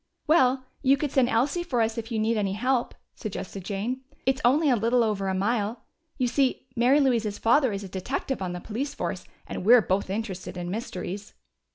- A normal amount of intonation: Yes, average, 4.5 semitones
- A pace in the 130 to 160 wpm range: No, average, 200 wpm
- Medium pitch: No, high, 230 Hz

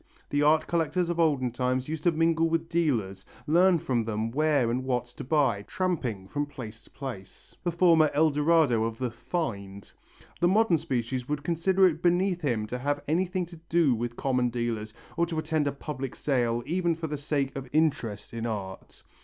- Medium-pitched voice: Yes, medium, 145 Hz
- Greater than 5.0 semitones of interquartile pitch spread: Yes, wide, 5.6 semitones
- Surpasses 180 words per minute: Yes, average, 190 wpm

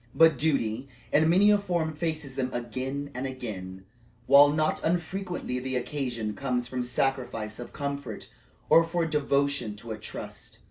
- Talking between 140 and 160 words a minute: Yes, average, 150 wpm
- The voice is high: No, medium, 140 Hz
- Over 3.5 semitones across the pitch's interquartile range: Yes, average, 4.3 semitones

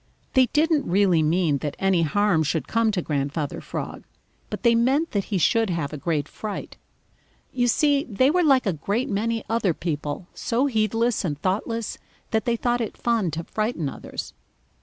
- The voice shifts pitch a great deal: Yes, wide, 6.1 semitones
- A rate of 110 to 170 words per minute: No, average, 180 wpm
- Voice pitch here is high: Yes, high, 210 Hz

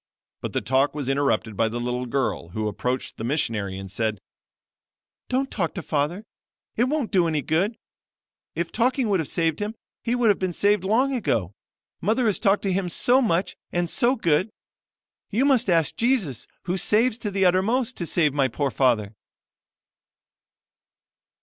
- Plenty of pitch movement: Yes, wide, 8.8 semitones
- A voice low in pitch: No, medium, 175 Hz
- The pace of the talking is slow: No, average, 170 wpm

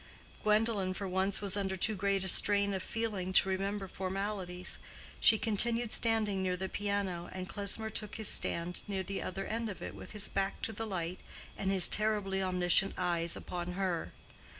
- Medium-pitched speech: No, high, 195 Hz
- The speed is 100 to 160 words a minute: No, average, 180 wpm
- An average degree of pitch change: No, narrow, 2.0 semitones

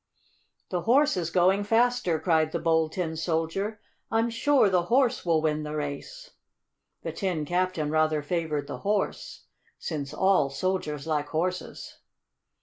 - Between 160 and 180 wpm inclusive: No, average, 145 wpm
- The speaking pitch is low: No, medium, 170 Hz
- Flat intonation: No, average, 4.3 semitones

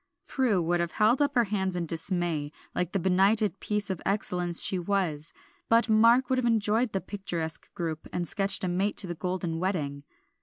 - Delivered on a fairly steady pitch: No, average, 3.6 semitones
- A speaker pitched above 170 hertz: Yes, high, 190 Hz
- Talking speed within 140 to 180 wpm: No, average, 190 wpm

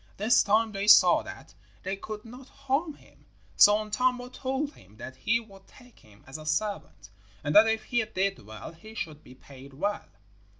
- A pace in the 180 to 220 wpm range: Yes, average, 185 wpm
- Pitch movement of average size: No, wide, 7.4 semitones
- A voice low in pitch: No, high, 210 Hz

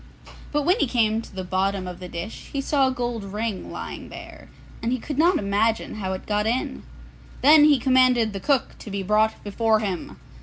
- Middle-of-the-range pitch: No, high, 220 Hz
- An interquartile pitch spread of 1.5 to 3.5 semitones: No, average, 4.5 semitones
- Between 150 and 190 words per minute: No, fast, 205 wpm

